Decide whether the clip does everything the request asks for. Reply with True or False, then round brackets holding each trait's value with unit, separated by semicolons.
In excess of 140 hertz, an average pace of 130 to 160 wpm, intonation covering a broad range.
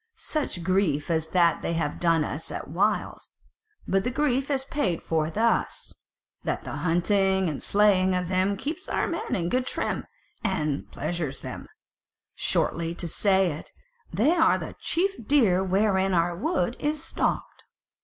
True (190 Hz; 155 wpm; 5.7 semitones)